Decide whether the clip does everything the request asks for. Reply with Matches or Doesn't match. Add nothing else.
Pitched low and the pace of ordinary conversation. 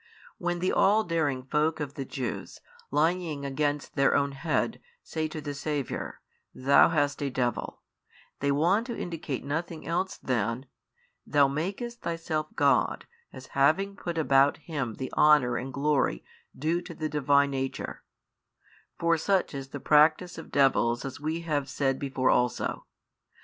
Doesn't match